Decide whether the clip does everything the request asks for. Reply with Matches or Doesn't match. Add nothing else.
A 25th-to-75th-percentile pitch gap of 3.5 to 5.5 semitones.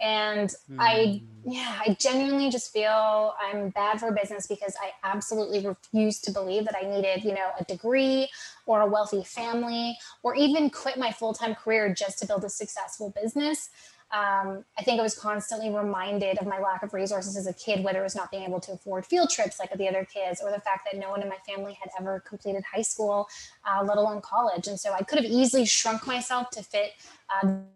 Doesn't match